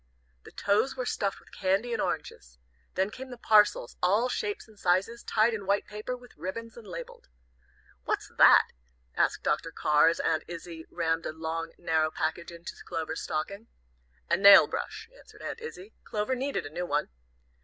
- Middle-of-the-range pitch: No, high, 200 Hz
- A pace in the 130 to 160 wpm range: No, average, 175 wpm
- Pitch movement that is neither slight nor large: No, wide, 5.7 semitones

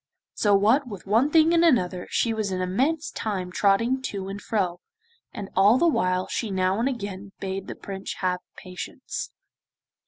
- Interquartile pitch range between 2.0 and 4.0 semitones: No, average, 4.6 semitones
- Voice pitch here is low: No, high, 200 Hz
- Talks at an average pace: Yes, average, 175 wpm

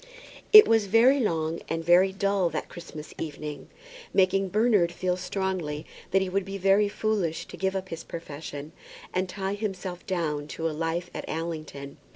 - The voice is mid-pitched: Yes, medium, 180 Hz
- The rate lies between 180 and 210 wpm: No, average, 170 wpm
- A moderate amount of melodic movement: Yes, average, 3.2 semitones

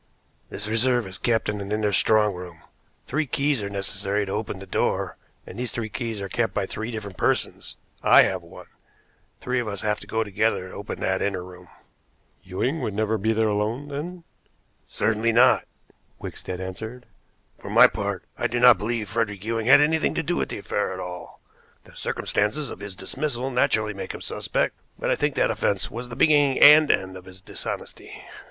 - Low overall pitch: Yes, low, 110 Hz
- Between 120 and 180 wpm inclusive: No, average, 195 wpm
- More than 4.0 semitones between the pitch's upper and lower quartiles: No, average, 3.7 semitones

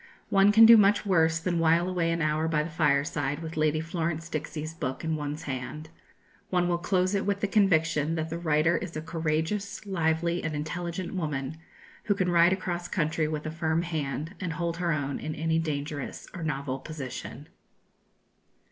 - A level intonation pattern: Yes, narrow, 2.3 semitones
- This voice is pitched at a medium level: Yes, medium, 160 Hz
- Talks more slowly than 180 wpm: No, average, 185 wpm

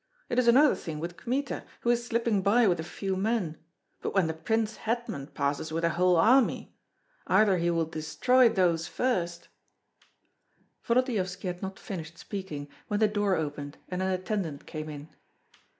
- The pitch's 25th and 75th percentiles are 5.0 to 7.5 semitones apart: Yes, wide, 5.5 semitones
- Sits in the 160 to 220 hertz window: Yes, medium, 185 Hz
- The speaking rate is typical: Yes, average, 170 wpm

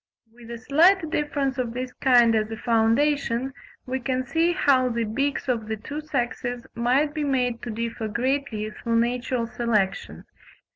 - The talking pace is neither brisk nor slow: Yes, average, 160 wpm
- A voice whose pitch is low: No, high, 245 Hz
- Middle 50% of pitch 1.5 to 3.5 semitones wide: Yes, average, 3.2 semitones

